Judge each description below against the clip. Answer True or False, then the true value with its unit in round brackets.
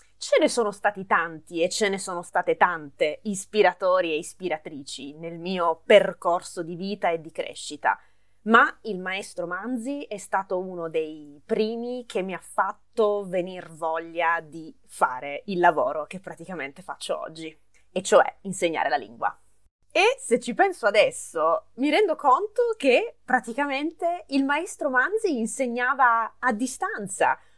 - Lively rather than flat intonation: True (6.7 semitones)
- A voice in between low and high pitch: False (195 Hz)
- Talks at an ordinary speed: True (145 wpm)